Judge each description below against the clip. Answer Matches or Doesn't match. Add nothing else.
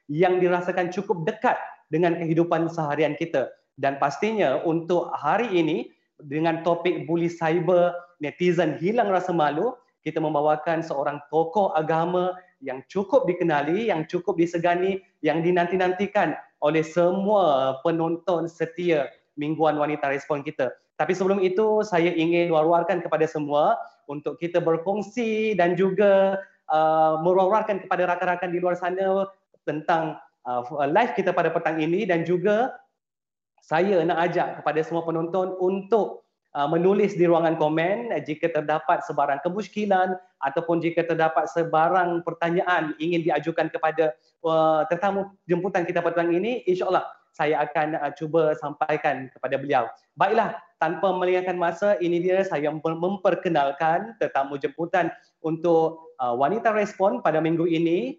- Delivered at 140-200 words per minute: Doesn't match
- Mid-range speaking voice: Matches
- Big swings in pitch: Doesn't match